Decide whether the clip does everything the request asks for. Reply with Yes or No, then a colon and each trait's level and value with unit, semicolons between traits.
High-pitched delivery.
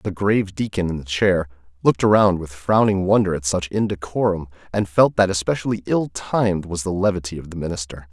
No: very low, 95 Hz